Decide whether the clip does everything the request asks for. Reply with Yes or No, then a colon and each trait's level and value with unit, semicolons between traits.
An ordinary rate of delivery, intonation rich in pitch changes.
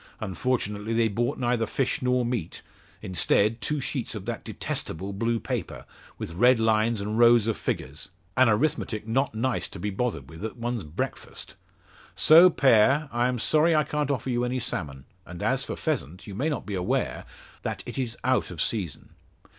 No: average, 180 wpm; average, 3.8 semitones